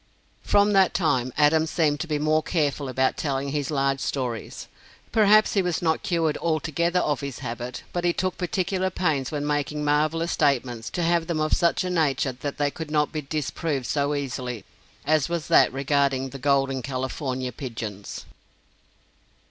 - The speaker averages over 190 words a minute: No, average, 170 wpm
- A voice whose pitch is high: No, medium, 150 Hz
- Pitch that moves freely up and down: No, average, 3.5 semitones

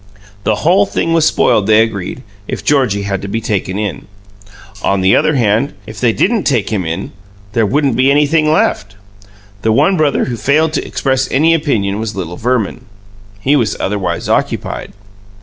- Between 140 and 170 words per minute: No, average, 180 wpm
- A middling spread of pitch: No, wide, 6.2 semitones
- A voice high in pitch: No, low, 115 Hz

